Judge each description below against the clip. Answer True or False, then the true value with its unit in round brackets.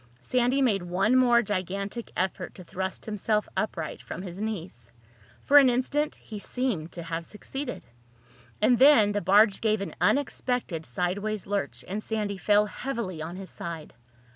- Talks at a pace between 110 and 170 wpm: True (155 wpm)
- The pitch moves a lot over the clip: False (4.6 semitones)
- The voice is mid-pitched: False (205 Hz)